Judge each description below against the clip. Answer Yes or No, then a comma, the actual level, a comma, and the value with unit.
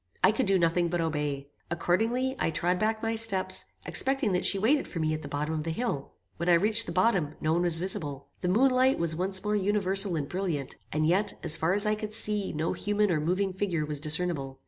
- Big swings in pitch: No, average, 4.8 semitones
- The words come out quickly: Yes, fast, 235 wpm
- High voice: No, medium, 180 Hz